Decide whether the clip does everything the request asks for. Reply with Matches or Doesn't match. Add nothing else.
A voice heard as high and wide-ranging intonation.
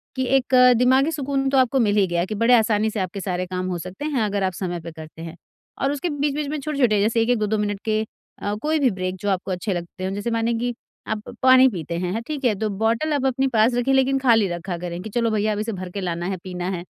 Matches